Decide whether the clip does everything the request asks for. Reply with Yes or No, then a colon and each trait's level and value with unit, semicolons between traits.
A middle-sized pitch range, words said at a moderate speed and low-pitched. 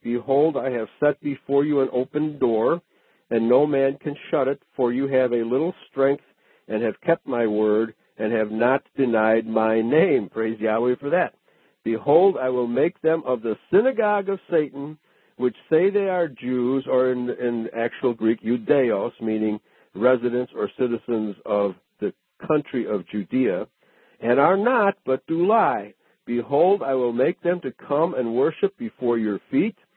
Yes: average, 4.2 semitones; average, 170 wpm; low, 125 Hz